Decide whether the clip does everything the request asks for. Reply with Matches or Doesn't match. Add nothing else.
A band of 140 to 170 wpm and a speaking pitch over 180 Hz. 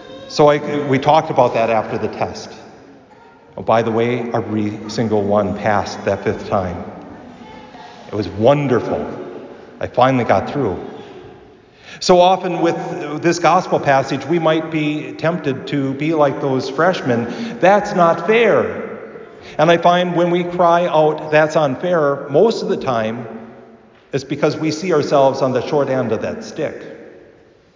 Doesn't match